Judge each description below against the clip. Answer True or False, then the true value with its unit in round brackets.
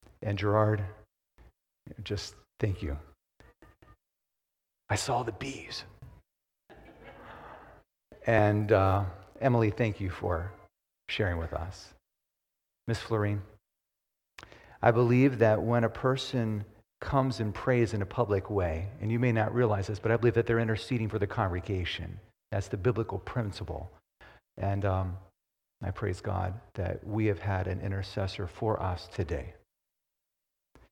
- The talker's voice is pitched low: True (105 Hz)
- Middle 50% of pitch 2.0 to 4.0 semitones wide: True (3.2 semitones)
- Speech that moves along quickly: False (130 wpm)